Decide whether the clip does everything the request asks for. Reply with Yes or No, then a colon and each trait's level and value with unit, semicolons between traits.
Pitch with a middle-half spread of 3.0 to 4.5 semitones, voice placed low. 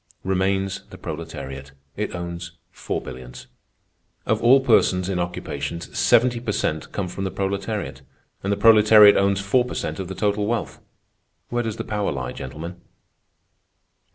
Yes: average, 3.7 semitones; very low, 95 Hz